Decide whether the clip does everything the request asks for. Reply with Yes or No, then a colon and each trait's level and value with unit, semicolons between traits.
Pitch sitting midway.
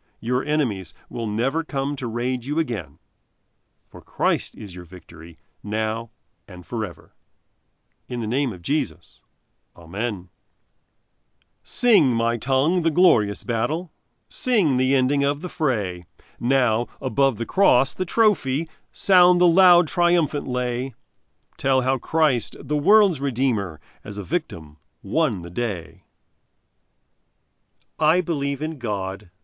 No: low, 125 Hz